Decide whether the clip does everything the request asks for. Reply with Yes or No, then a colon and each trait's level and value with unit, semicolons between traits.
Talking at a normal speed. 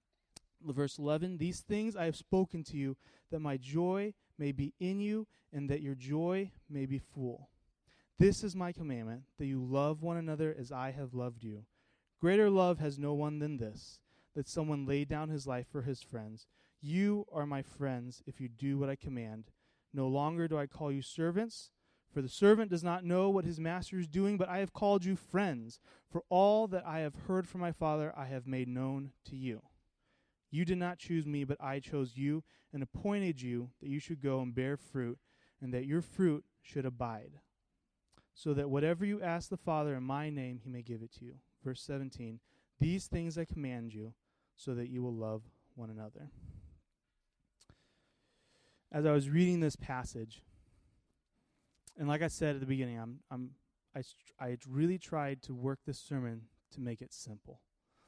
Yes: average, 190 wpm